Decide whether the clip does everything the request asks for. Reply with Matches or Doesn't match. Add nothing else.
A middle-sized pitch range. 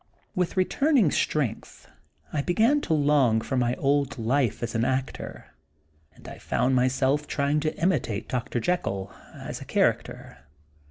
Matches